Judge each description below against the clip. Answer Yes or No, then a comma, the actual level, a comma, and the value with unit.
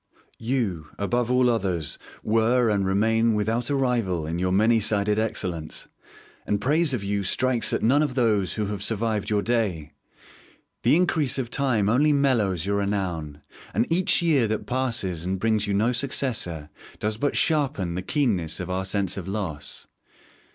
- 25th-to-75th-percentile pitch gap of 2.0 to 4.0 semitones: No, average, 4.6 semitones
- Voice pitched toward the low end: Yes, low, 110 Hz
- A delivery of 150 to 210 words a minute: Yes, average, 165 wpm